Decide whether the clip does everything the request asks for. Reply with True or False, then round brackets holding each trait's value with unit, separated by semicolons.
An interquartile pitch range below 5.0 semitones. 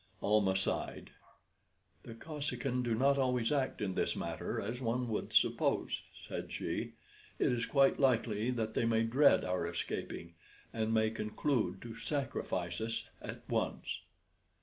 True (3.1 semitones)